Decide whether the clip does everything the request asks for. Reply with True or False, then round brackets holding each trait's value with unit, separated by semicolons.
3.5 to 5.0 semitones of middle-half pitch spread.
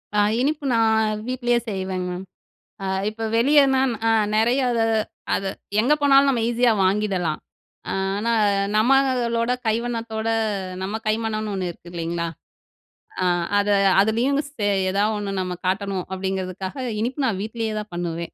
True (3.8 semitones)